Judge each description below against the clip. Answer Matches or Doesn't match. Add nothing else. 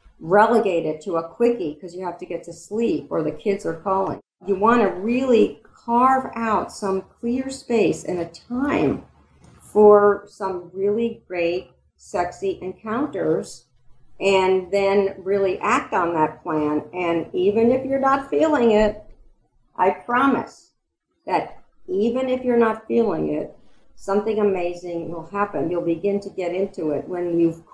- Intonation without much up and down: Doesn't match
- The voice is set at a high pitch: Matches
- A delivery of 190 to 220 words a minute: Doesn't match